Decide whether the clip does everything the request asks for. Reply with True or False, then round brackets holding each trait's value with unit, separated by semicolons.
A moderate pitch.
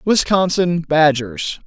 True (165 Hz)